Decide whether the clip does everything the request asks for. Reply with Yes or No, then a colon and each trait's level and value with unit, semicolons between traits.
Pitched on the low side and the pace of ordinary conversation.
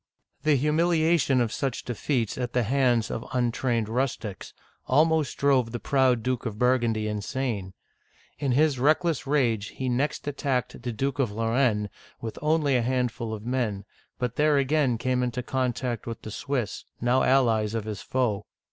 Yes: low, 125 Hz; average, 160 wpm